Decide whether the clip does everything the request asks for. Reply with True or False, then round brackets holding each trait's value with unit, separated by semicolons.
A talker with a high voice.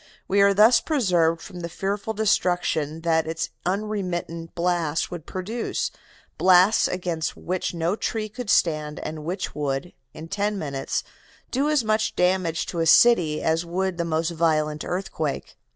False (175 Hz)